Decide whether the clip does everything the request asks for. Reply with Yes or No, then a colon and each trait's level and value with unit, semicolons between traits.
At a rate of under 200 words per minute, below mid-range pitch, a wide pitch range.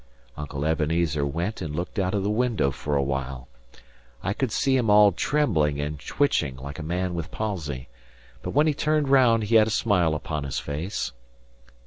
Yes: average, 180 wpm; very low, 85 Hz; wide, 7.0 semitones